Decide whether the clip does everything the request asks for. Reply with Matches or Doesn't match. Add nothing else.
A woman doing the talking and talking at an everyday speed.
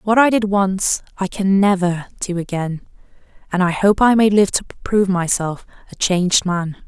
Matches